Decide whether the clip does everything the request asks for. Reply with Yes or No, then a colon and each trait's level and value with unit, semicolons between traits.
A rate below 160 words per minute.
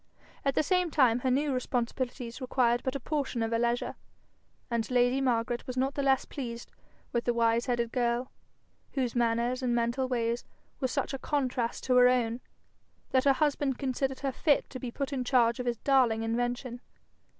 No: average, 185 wpm